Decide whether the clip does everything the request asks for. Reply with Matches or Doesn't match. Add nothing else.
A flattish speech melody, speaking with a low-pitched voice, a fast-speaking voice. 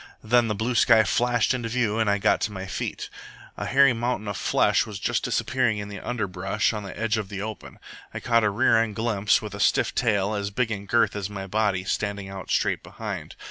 Matches